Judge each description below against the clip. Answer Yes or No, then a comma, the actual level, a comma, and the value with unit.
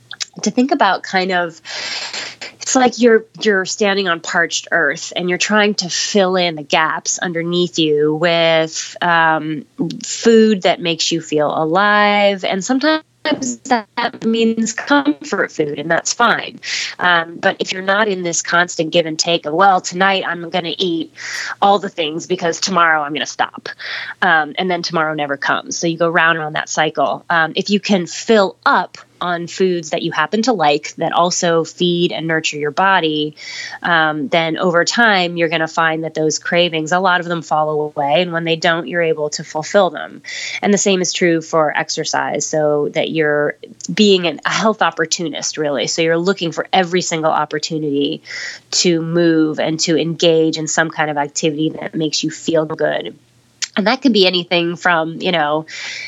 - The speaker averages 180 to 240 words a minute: Yes, average, 185 wpm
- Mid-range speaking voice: Yes, medium, 170 Hz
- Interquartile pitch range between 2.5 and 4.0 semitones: Yes, average, 3.4 semitones